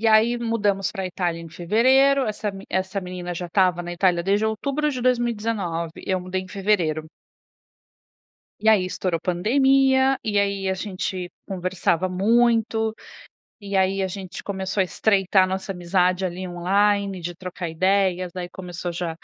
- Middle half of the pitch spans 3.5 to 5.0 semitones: No, average, 2.9 semitones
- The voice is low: No, high, 190 Hz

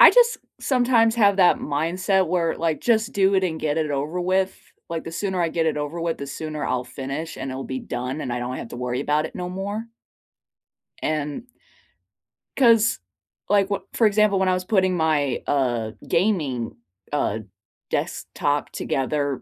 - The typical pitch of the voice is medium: Yes, medium, 165 Hz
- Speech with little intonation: No, average, 5.2 semitones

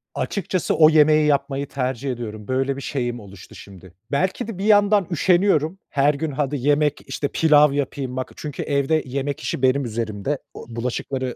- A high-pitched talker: No, medium, 140 Hz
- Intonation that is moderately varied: Yes, average, 3.2 semitones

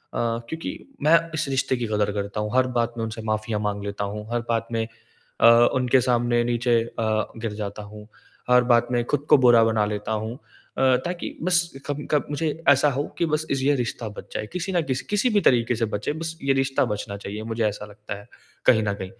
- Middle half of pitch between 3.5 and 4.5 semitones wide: Yes, average, 4.0 semitones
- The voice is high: No, low, 120 Hz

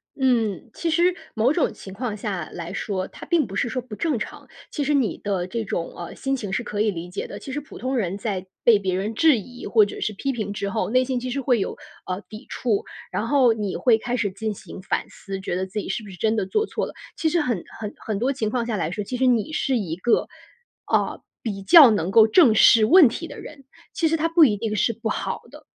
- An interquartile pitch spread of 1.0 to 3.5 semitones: No, average, 4.5 semitones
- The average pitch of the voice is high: Yes, high, 220 Hz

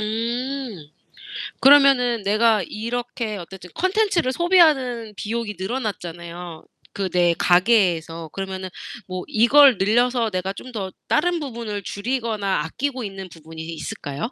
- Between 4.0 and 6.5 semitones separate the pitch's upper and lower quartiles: Yes, average, 5.3 semitones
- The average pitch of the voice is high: Yes, high, 215 Hz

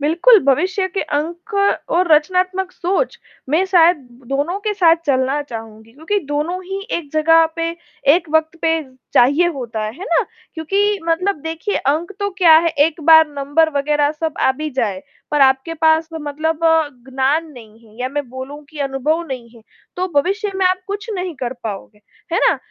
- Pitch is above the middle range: Yes, very high, 320 Hz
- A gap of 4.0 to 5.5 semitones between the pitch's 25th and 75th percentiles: Yes, average, 4.3 semitones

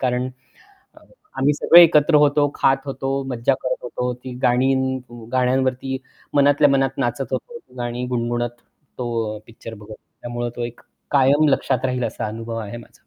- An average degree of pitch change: No, narrow, 2.3 semitones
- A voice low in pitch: Yes, low, 130 Hz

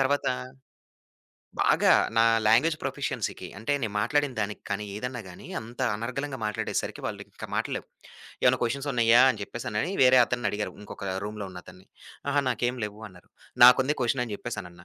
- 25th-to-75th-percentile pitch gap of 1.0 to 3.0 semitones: No, average, 3.8 semitones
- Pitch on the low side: Yes, low, 115 Hz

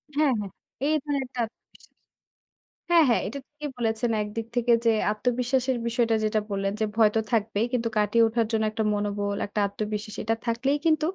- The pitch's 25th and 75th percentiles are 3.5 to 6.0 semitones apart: No, average, 3.0 semitones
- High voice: Yes, high, 230 Hz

